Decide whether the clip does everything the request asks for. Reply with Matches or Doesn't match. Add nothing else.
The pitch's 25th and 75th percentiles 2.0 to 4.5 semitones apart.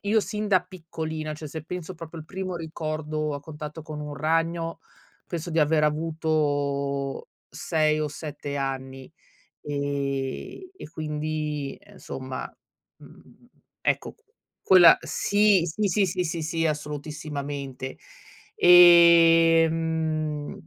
Matches